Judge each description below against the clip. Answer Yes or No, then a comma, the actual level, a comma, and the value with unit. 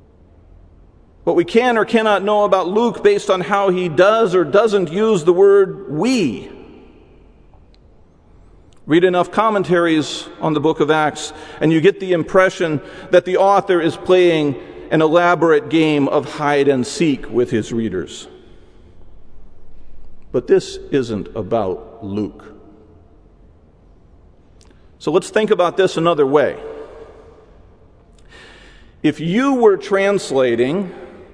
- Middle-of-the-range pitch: Yes, medium, 165 Hz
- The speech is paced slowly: Yes, slow, 120 wpm